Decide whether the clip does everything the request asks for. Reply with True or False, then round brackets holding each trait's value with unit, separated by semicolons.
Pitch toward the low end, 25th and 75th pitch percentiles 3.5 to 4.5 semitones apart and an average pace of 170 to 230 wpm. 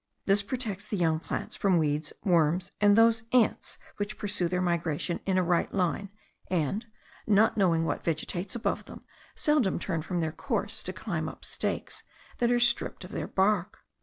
False (190 Hz; 3.9 semitones; 175 wpm)